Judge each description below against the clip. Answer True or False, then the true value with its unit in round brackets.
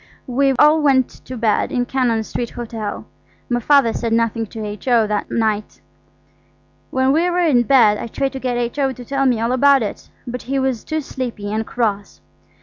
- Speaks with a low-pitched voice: False (245 Hz)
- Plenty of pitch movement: False (3.2 semitones)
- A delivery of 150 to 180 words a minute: False (190 wpm)